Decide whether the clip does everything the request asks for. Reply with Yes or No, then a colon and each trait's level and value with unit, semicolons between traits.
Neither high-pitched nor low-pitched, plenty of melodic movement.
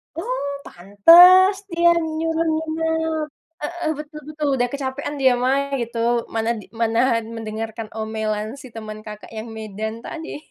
No: very high, 270 Hz; wide, 6.5 semitones